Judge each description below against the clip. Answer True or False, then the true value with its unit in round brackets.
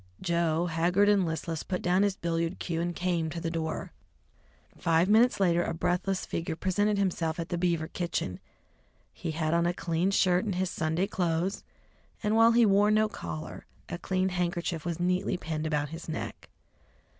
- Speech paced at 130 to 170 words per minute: False (180 wpm)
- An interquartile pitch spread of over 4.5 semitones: False (2.4 semitones)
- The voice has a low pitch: False (175 Hz)